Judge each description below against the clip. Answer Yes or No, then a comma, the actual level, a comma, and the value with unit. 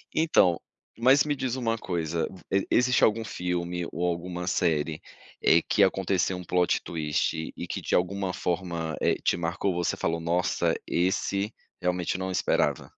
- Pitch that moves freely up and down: No, narrow, 2.5 semitones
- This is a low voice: Yes, very low, 90 Hz